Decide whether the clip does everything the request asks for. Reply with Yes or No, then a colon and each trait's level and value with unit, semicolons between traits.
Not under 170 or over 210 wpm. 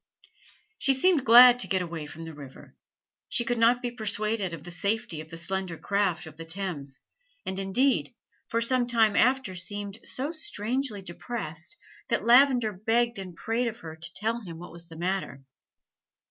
Yes: average, 175 wpm